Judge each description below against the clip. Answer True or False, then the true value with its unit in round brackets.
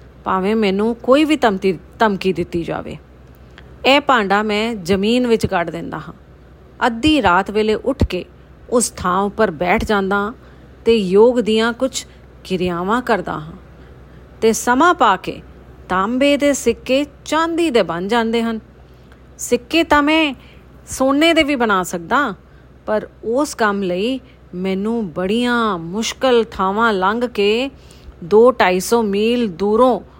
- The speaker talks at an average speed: False (130 wpm)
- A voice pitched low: False (220 Hz)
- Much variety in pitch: False (4.7 semitones)